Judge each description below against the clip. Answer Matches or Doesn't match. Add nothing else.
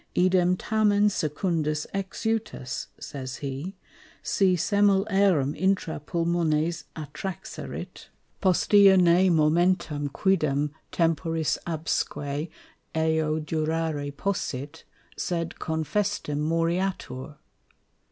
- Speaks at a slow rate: Matches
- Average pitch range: Matches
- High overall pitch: Doesn't match